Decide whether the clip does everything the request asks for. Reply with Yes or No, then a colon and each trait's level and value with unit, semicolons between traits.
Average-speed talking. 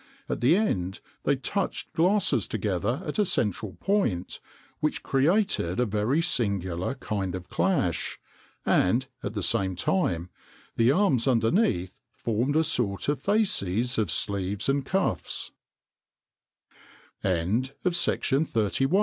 No: slow, 110 wpm